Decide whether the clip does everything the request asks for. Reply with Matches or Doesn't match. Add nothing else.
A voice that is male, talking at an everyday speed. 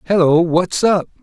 Matches